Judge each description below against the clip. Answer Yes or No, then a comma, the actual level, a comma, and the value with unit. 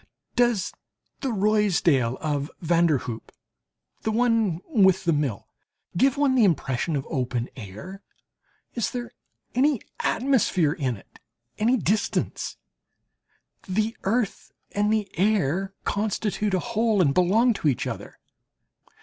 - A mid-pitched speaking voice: No, high, 195 Hz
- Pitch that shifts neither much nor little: No, wide, 6.5 semitones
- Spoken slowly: Yes, slow, 125 wpm